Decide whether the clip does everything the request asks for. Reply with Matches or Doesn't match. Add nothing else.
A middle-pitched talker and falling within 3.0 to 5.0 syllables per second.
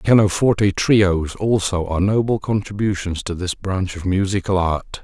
Doesn't match